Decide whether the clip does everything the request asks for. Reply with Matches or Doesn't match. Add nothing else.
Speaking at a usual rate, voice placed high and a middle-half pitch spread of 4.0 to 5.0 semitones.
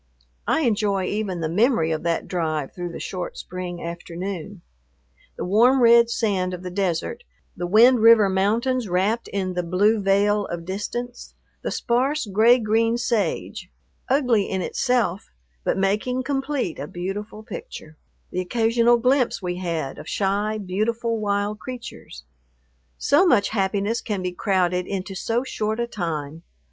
Matches